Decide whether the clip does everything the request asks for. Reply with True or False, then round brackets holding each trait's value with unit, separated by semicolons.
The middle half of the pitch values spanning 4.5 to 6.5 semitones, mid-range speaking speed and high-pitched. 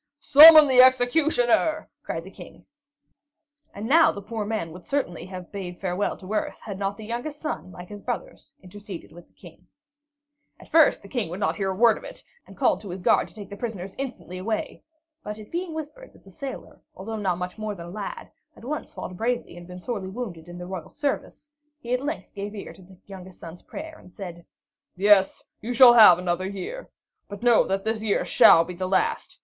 False (5.1 semitones; 215 wpm; 205 Hz)